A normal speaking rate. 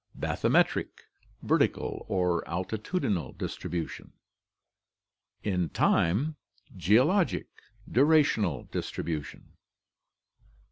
No: slow, 55 wpm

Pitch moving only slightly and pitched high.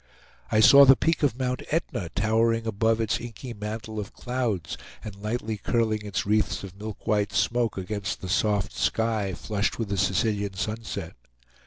No: narrow, 2.2 semitones; low, 110 Hz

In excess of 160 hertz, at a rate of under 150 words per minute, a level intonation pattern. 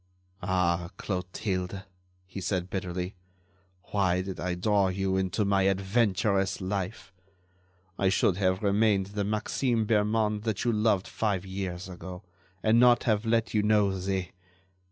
No: very low, 95 Hz; slow, 135 wpm; narrow, 2.3 semitones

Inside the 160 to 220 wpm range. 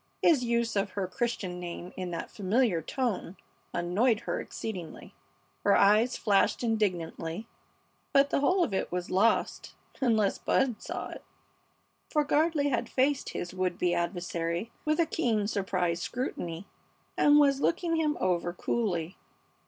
No: average, 145 wpm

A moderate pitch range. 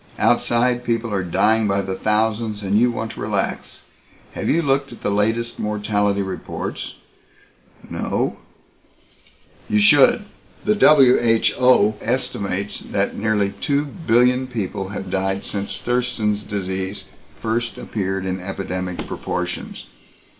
Yes: average, 3.5 semitones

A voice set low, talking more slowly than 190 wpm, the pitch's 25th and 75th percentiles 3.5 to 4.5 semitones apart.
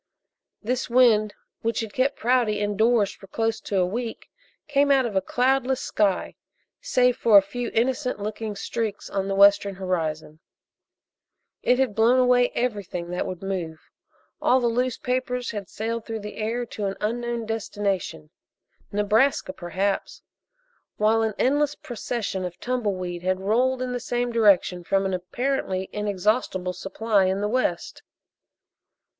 No: high, 215 Hz; average, 150 wpm; average, 4.0 semitones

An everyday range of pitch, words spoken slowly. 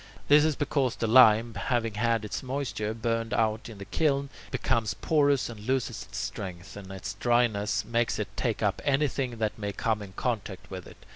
No: average, 3.7 semitones; average, 190 wpm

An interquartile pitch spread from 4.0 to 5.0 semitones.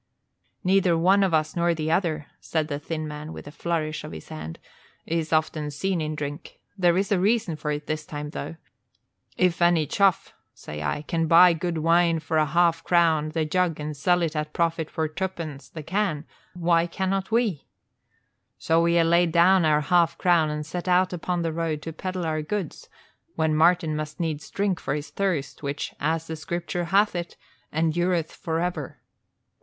No: narrow, 2.4 semitones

